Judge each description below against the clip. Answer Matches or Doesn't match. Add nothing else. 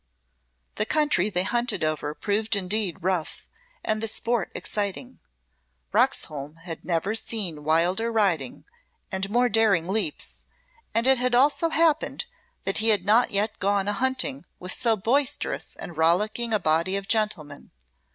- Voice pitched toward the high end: Matches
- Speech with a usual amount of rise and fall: Matches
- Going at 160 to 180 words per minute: Doesn't match